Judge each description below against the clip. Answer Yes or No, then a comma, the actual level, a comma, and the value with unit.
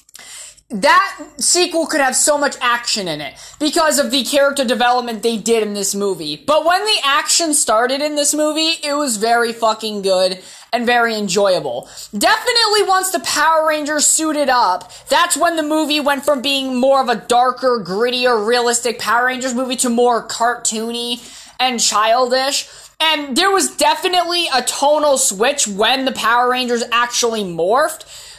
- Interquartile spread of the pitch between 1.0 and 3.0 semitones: No, average, 4.3 semitones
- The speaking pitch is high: Yes, very high, 260 Hz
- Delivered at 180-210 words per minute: No, average, 160 wpm